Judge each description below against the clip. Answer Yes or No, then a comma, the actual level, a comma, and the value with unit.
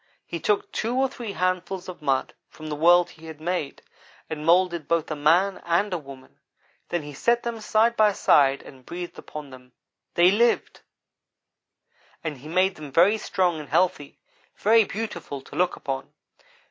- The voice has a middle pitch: Yes, medium, 175 Hz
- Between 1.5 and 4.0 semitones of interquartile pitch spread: No, average, 4.6 semitones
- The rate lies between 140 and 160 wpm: No, average, 170 wpm